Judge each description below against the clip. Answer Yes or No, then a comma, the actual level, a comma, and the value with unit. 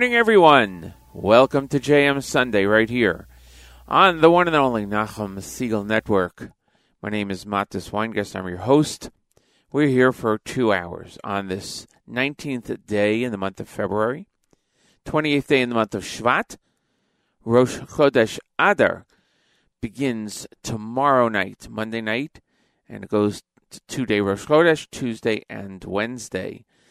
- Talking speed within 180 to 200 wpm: No, average, 145 wpm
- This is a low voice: Yes, low, 110 Hz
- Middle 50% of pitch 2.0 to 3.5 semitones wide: No, average, 5.1 semitones